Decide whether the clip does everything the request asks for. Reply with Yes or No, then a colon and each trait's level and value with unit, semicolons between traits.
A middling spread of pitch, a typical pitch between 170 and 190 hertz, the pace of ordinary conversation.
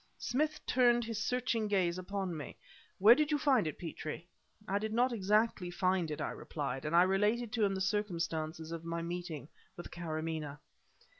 Yes: average, 5.0 semitones; medium, 185 Hz; average, 175 wpm